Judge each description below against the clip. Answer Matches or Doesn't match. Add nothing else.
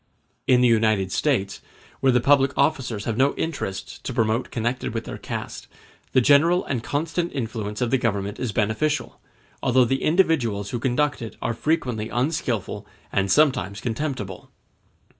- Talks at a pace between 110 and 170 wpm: Matches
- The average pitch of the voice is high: Doesn't match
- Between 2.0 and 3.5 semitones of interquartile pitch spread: Doesn't match